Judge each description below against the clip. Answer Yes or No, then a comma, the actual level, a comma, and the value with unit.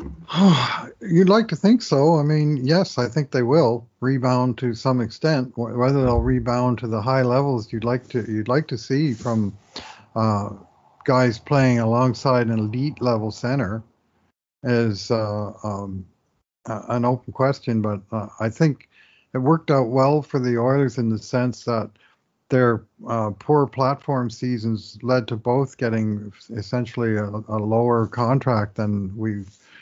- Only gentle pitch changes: No, average, 3.2 semitones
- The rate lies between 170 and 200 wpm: No, average, 155 wpm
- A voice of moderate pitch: No, low, 120 Hz